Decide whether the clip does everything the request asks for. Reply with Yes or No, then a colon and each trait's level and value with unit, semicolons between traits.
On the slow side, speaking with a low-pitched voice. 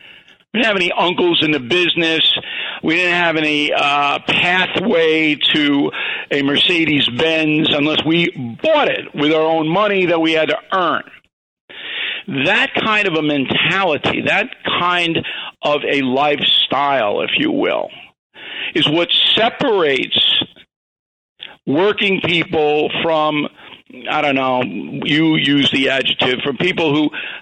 No: slow, 130 wpm; medium, 160 Hz